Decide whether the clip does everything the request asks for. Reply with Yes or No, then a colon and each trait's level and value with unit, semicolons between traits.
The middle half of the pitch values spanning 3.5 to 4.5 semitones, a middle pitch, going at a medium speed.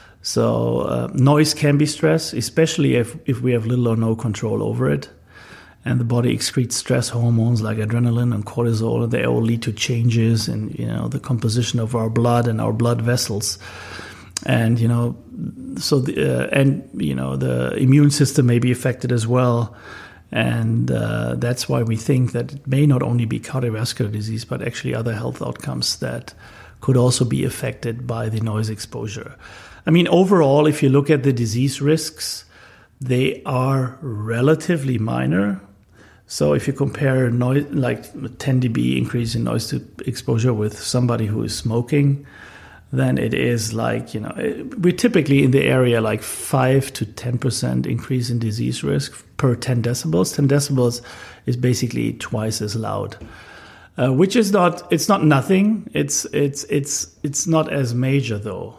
No: average, 3.8 semitones; low, 120 Hz; average, 170 wpm